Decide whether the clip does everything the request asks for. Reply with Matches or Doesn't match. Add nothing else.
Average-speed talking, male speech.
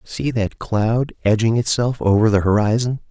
Matches